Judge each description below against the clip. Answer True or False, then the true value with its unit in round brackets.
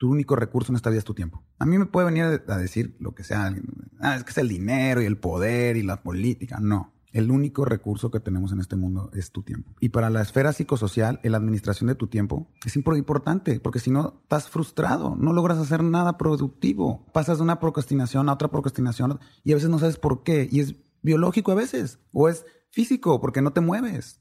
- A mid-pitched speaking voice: False (130 Hz)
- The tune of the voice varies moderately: False (5.8 semitones)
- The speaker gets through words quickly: True (225 wpm)